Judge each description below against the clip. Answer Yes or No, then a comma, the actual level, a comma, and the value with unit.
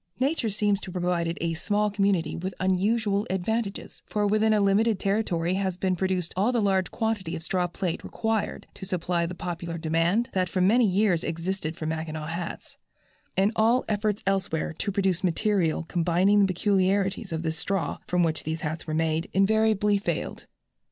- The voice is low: No, high, 190 Hz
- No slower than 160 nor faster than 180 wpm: Yes, average, 175 wpm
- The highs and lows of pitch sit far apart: No, average, 3.5 semitones